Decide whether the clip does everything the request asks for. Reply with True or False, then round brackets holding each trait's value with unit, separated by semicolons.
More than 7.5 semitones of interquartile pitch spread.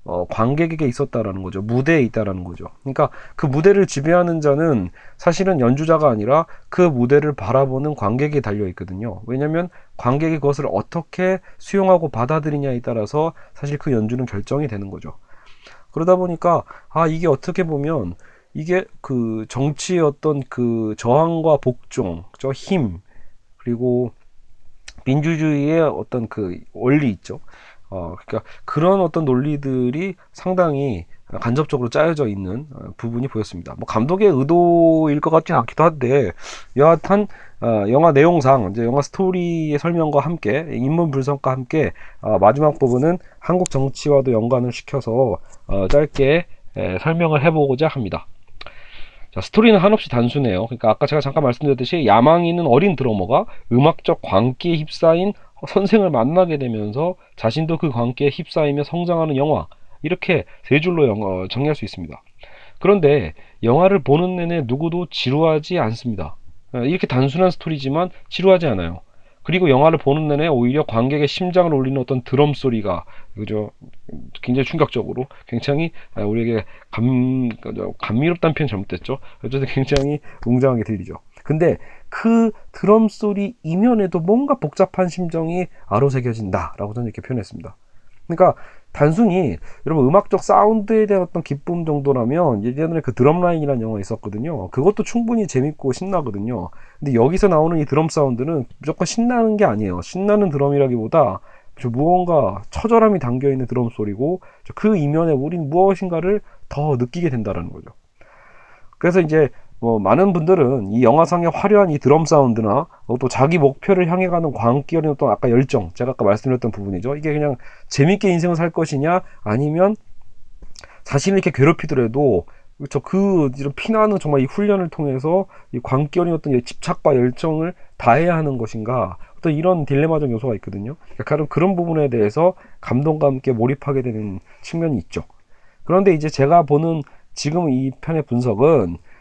False (5.9 semitones)